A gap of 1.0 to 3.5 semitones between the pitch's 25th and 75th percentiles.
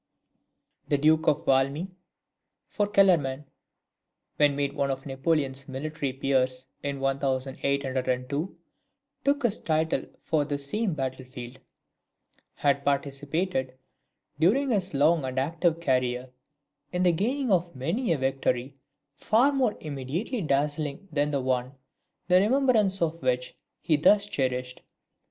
No: average, 4.9 semitones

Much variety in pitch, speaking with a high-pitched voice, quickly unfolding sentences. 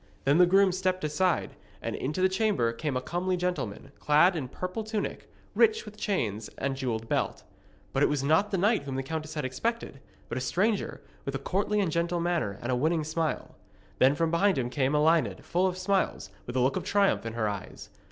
No: wide, 6.0 semitones; medium, 160 Hz; fast, 210 wpm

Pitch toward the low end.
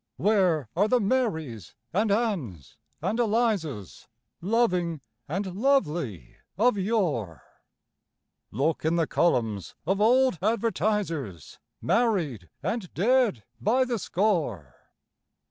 No: medium, 185 Hz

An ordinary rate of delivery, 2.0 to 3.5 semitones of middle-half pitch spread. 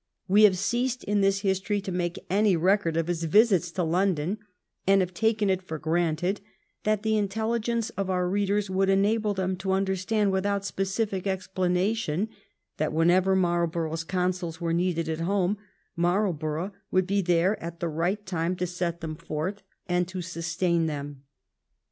Yes: average, 170 wpm; average, 2.8 semitones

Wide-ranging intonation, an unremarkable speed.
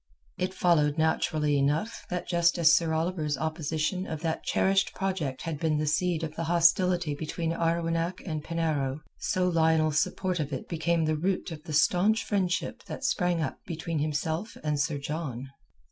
No: narrow, 2.4 semitones; average, 170 wpm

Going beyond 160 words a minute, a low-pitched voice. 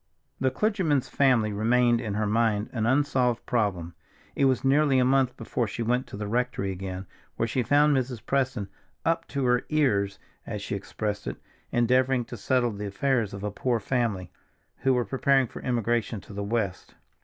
Yes: average, 180 wpm; low, 120 Hz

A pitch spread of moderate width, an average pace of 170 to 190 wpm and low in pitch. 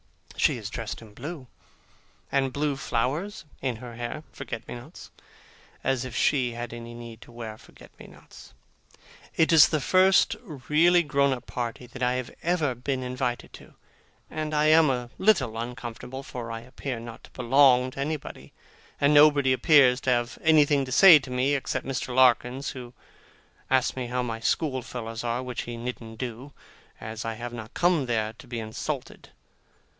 Yes: average, 3.2 semitones; average, 175 wpm; low, 125 Hz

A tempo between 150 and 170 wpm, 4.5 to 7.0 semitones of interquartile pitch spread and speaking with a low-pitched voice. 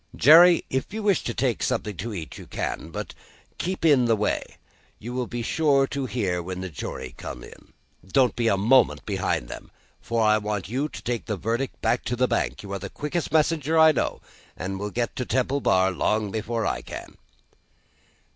No: fast, 205 wpm; average, 4.9 semitones; low, 120 Hz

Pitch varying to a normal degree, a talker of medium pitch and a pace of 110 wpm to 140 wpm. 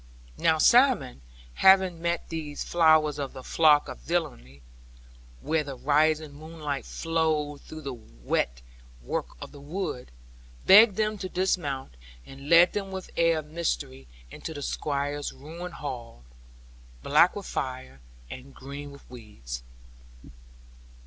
Yes: average, 3.8 semitones; medium, 150 Hz; slow, 135 wpm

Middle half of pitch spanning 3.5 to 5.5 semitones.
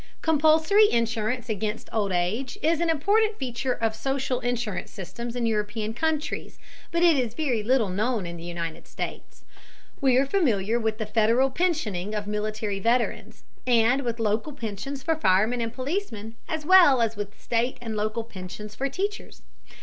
Yes: average, 4.5 semitones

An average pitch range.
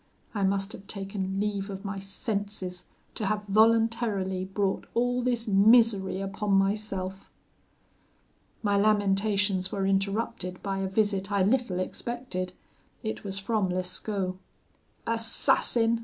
No: narrow, 2.1 semitones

